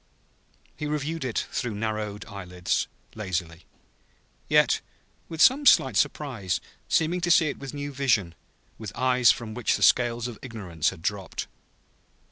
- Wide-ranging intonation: Yes, wide, 6.0 semitones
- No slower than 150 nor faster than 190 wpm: No, slow, 135 wpm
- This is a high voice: No, low, 115 Hz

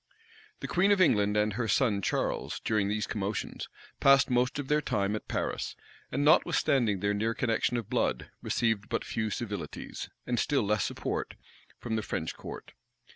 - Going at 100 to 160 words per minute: No, average, 170 wpm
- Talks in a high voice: No, low, 110 Hz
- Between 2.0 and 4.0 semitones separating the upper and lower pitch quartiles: Yes, average, 3.6 semitones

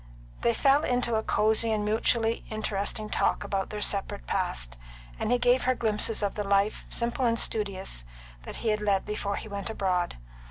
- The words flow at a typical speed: Yes, average, 175 wpm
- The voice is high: Yes, high, 215 Hz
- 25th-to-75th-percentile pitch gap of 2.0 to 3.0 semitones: Yes, narrow, 2.5 semitones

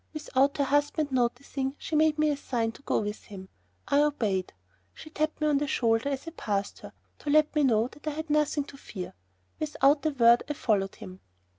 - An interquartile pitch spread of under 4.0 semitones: No, average, 4.8 semitones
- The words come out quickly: Yes, fast, 210 wpm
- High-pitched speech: Yes, very high, 280 Hz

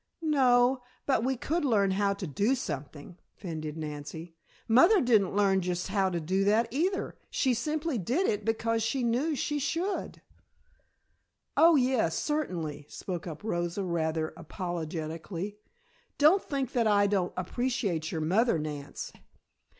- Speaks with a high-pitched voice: Yes, high, 205 Hz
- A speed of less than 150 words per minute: Yes, average, 140 wpm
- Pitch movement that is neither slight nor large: No, wide, 7.1 semitones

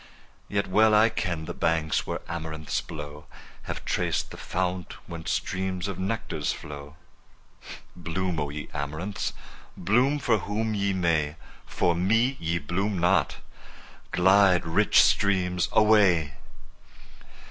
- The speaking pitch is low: Yes, very low, 90 Hz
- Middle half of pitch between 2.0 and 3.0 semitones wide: No, average, 3.7 semitones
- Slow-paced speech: Yes, slow, 125 wpm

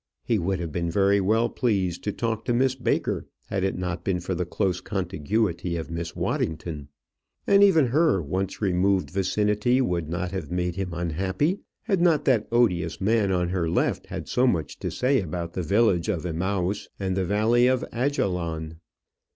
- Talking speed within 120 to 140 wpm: No, average, 180 wpm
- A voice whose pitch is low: Yes, very low, 95 Hz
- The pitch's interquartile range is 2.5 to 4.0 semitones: No, average, 4.6 semitones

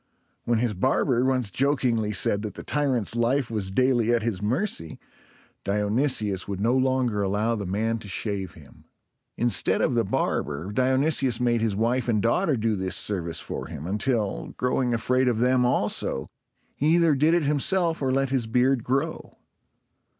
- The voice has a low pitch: Yes, low, 120 Hz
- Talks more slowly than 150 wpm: No, average, 165 wpm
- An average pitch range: Yes, average, 4.1 semitones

